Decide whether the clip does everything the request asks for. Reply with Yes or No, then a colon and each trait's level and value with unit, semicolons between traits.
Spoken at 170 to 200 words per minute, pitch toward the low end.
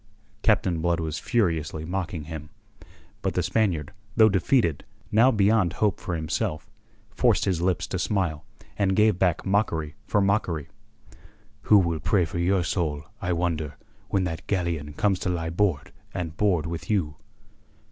No: average, 155 wpm; very low, 90 Hz